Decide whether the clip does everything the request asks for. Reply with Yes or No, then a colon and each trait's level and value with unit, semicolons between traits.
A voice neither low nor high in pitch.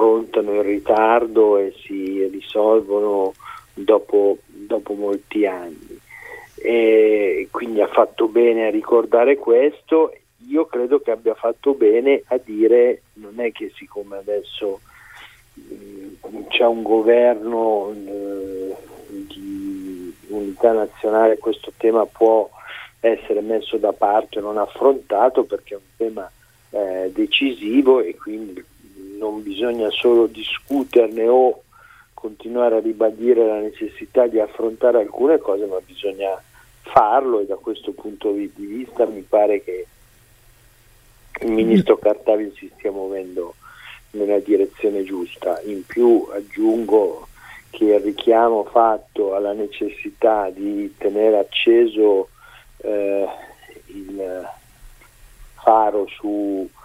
No: low, 120 Hz